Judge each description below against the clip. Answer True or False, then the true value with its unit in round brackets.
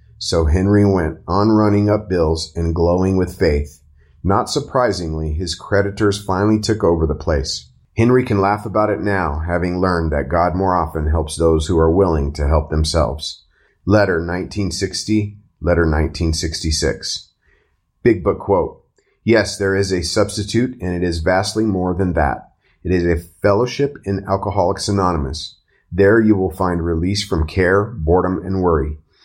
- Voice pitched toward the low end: True (90 Hz)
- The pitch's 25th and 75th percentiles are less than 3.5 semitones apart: False (3.8 semitones)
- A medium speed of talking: True (155 wpm)